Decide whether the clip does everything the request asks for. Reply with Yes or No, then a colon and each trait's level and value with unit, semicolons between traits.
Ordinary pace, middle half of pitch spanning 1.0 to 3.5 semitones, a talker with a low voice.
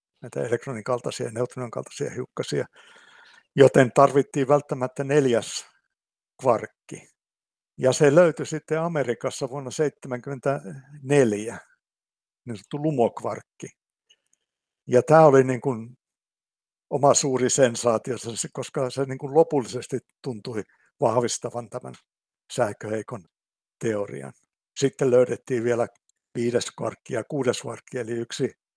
Yes: average, 105 wpm; average, 2.9 semitones; low, 130 Hz